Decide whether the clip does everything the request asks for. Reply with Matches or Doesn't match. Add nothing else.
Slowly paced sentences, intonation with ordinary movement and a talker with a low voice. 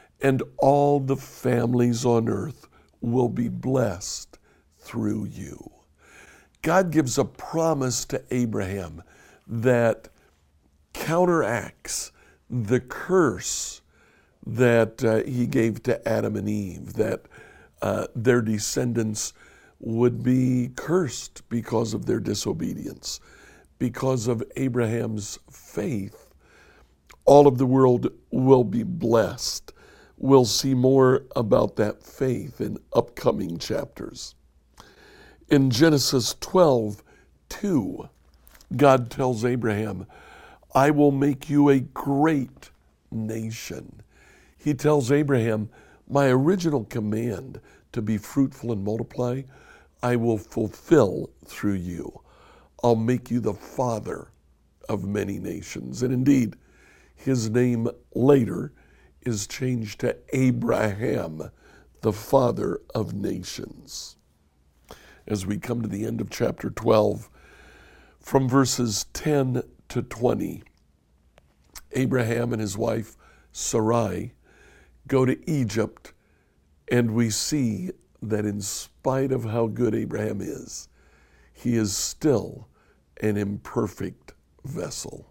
Matches